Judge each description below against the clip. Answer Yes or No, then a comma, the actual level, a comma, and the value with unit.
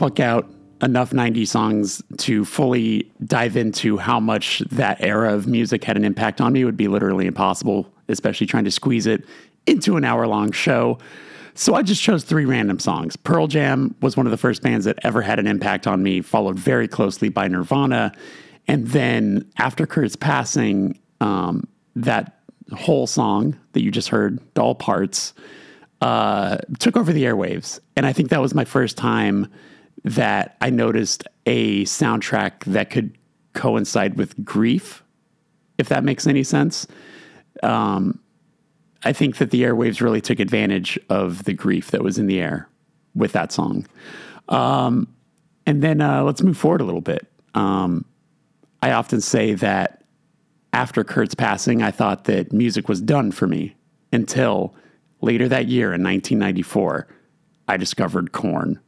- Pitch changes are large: No, average, 5.0 semitones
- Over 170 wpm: No, average, 160 wpm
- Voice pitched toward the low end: Yes, low, 115 Hz